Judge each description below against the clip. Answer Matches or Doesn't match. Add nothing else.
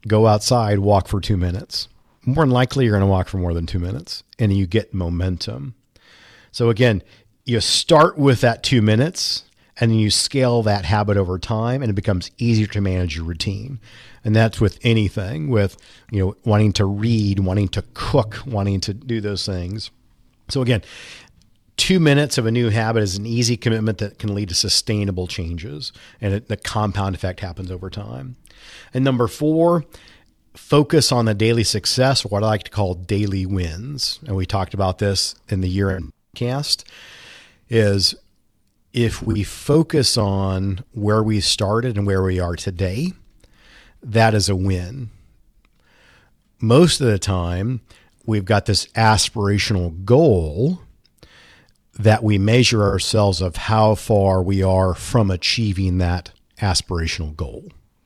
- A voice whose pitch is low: Matches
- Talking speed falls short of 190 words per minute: Matches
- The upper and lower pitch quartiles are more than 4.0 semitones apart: Doesn't match